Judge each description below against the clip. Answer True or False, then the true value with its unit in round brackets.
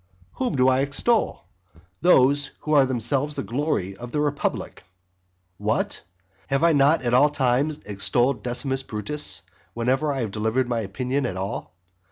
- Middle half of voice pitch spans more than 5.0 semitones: False (3.4 semitones)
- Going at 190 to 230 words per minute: False (155 wpm)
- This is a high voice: False (130 Hz)